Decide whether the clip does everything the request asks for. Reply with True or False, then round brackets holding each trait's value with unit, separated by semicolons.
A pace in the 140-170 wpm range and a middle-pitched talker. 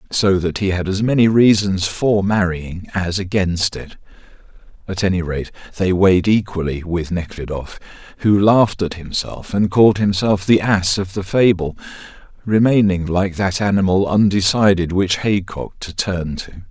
False (150 wpm; 95 Hz)